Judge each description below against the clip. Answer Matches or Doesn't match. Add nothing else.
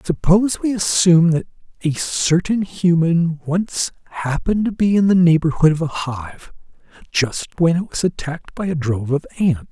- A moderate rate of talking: Matches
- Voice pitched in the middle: Matches